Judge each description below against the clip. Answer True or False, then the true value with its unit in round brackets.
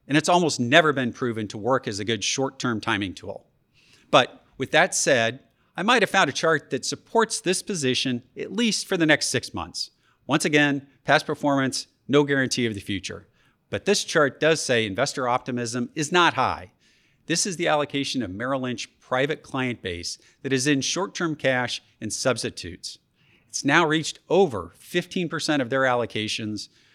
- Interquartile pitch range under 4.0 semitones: False (4.3 semitones)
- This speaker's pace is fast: False (180 wpm)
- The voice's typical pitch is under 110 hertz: False (135 Hz)